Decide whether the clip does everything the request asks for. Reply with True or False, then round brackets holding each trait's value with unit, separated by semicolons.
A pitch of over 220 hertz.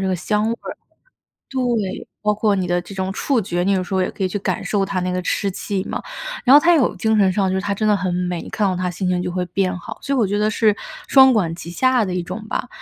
False (195 Hz)